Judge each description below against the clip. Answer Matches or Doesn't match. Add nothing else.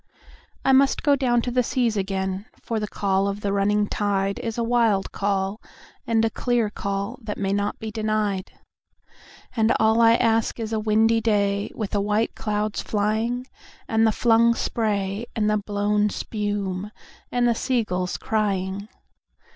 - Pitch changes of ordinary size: Doesn't match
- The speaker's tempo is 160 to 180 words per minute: Matches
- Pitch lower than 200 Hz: Doesn't match